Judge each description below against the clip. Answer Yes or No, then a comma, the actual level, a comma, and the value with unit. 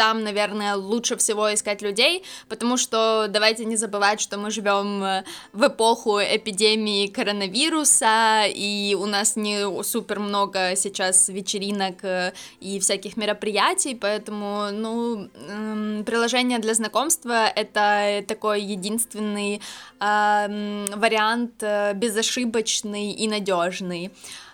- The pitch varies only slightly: Yes, narrow, 1.7 semitones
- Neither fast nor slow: No, slow, 100 wpm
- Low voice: No, high, 210 Hz